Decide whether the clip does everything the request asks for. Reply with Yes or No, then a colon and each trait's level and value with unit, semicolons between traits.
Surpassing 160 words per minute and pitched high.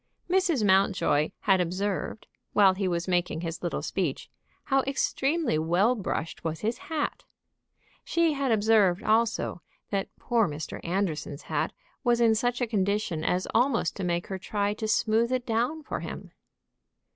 No: average, 155 wpm; high, 205 Hz